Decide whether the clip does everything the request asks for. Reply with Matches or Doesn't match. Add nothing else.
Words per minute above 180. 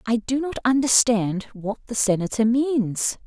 Doesn't match